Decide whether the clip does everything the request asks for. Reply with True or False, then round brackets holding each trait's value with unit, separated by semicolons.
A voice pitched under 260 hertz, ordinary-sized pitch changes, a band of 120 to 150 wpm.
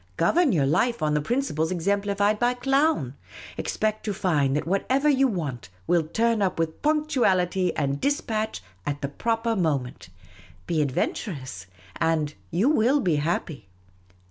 False (185 Hz; 7.6 semitones; 145 wpm)